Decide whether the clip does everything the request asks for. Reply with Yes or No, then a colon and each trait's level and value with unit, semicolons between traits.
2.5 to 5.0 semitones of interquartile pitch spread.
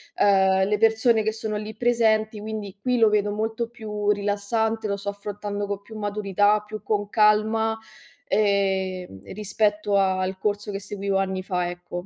No: narrow, 1.6 semitones